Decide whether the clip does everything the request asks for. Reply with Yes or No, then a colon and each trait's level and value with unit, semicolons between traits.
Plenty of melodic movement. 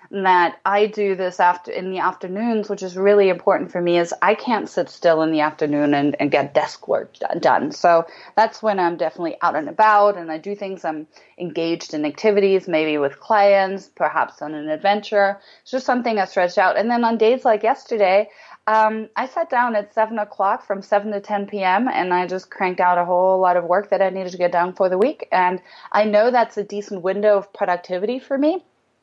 No: average, 3.1 semitones